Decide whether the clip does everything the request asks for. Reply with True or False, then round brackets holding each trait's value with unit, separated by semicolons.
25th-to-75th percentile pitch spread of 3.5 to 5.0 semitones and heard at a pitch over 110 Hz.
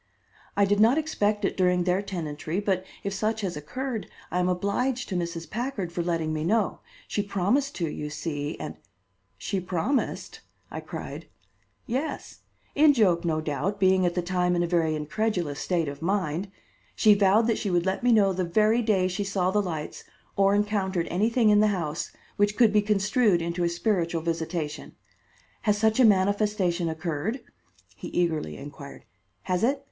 True (3.8 semitones; 190 Hz)